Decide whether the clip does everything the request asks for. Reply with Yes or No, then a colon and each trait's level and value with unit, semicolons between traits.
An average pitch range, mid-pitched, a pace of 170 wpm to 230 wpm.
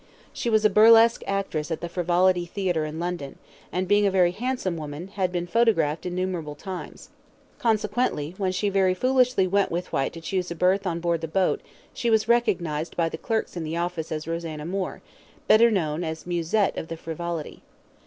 Yes: average, 3.5 semitones; medium, 180 Hz; average, 190 wpm